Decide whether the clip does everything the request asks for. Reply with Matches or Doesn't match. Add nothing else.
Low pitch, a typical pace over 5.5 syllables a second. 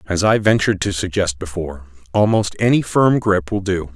Doesn't match